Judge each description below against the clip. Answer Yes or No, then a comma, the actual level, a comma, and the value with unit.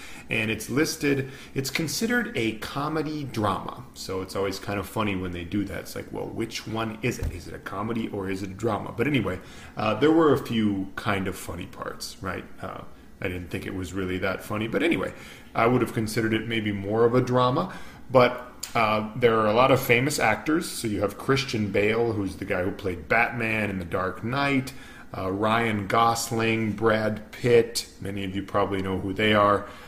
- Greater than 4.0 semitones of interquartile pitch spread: No, average, 3.5 semitones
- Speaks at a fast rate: Yes, fast, 210 wpm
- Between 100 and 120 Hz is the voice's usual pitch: Yes, low, 110 Hz